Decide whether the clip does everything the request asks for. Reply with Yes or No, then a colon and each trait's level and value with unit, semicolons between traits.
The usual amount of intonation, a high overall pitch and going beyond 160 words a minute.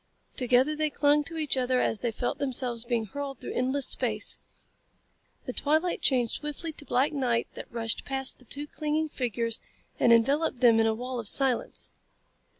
Yes: average, 3.5 semitones; very high, 260 Hz; average, 175 wpm